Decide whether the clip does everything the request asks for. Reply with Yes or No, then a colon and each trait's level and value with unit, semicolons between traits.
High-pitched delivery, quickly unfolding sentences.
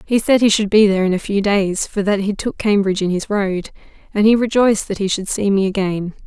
Yes: high, 200 Hz; fast, 260 wpm